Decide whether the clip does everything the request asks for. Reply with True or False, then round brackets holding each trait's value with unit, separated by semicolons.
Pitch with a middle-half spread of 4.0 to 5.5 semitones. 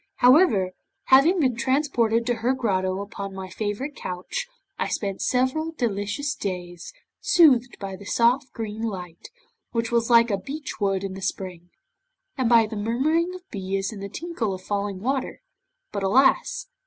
True (5.2 semitones)